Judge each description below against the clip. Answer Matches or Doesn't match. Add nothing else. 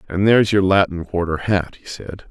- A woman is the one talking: Doesn't match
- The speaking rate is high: Matches